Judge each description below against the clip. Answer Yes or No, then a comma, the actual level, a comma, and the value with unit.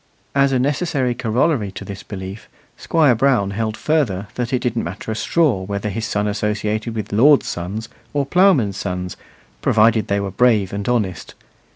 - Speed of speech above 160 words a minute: Yes, average, 170 wpm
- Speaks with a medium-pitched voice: No, low, 110 Hz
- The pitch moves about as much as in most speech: Yes, average, 4.3 semitones